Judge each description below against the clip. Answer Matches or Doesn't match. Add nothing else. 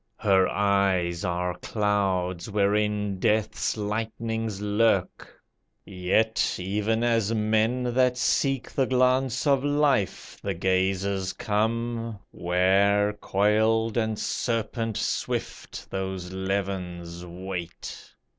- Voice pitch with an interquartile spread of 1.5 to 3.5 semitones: Matches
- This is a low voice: Matches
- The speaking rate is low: Matches